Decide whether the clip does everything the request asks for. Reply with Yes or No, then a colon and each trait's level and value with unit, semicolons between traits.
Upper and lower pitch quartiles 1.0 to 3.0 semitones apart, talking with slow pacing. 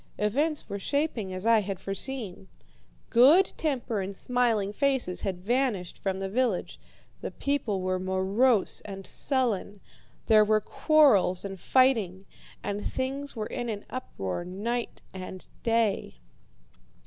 No: average, 5.1 semitones; slow, 130 wpm